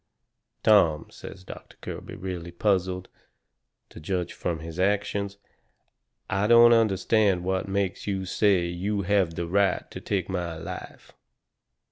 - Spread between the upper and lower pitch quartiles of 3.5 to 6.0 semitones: No, narrow, 2.4 semitones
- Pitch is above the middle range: No, very low, 95 Hz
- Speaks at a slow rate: Yes, slow, 130 wpm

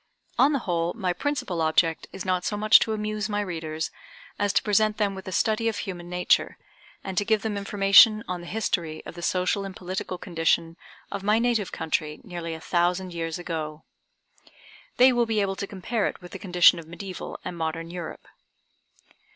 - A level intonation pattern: No, average, 3.5 semitones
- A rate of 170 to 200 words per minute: Yes, average, 190 wpm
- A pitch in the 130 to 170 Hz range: No, medium, 185 Hz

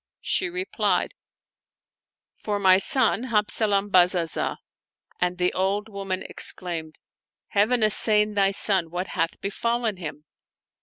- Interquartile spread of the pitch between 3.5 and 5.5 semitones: No, average, 3.0 semitones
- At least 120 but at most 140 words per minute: Yes, slow, 135 wpm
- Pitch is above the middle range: Yes, high, 200 Hz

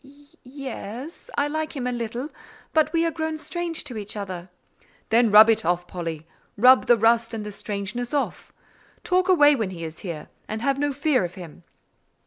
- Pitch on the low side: No, high, 240 Hz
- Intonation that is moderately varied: No, wide, 6.3 semitones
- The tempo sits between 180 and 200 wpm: Yes, average, 185 wpm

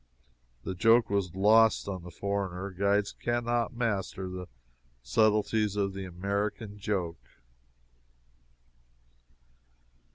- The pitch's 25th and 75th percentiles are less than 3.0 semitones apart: Yes, narrow, 2.5 semitones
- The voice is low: Yes, low, 100 Hz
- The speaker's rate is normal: No, slow, 100 wpm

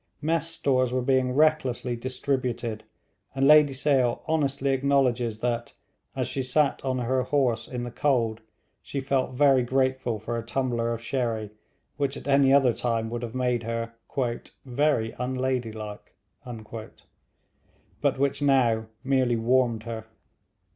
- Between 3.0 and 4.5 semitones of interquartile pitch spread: No, narrow, 2.6 semitones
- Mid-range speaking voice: No, low, 125 Hz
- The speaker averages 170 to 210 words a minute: No, slow, 135 wpm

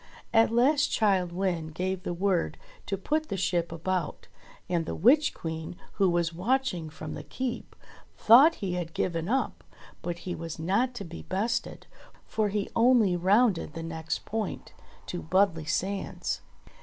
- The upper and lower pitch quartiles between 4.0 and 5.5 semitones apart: Yes, average, 4.9 semitones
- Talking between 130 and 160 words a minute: Yes, average, 155 wpm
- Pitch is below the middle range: No, medium, 185 Hz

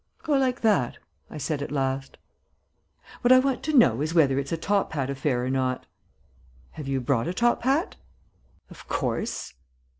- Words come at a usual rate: Yes, average, 175 wpm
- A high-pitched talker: No, medium, 150 Hz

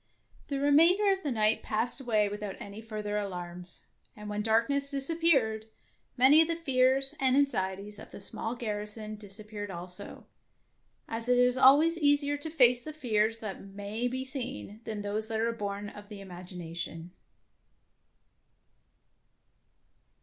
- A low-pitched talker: No, high, 220 Hz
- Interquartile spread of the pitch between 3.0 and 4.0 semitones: No, average, 4.7 semitones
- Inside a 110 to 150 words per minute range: Yes, average, 140 wpm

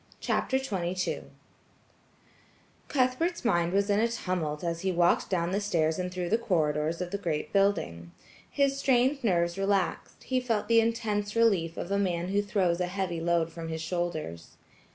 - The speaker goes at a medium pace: Yes, average, 170 wpm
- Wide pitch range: No, average, 4.1 semitones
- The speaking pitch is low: No, medium, 185 Hz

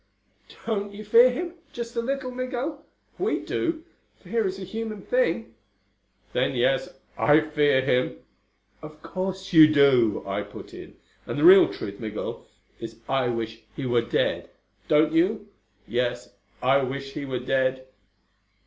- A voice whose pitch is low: No, medium, 155 Hz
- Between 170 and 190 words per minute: No, average, 150 wpm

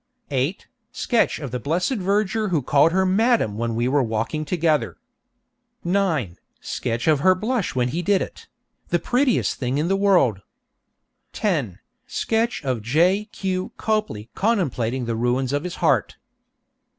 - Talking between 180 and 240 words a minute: No, average, 150 wpm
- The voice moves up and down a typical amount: No, wide, 7.9 semitones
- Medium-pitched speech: Yes, medium, 160 Hz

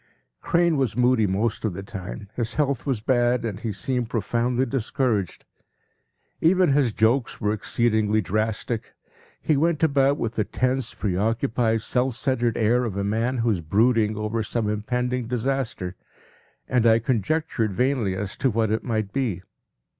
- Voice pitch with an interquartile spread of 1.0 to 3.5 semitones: Yes, average, 3.2 semitones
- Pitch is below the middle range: Yes, low, 115 Hz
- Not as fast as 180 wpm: Yes, average, 160 wpm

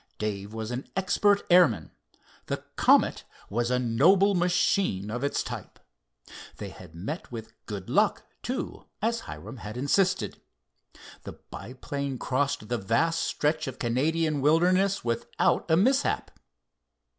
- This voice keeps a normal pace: No, slow, 125 wpm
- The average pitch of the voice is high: No, medium, 140 Hz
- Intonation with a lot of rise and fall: Yes, wide, 7.6 semitones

